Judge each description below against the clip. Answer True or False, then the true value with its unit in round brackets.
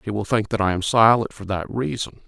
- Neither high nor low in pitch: False (105 Hz)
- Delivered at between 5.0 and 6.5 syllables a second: True (5.7 syllables/s)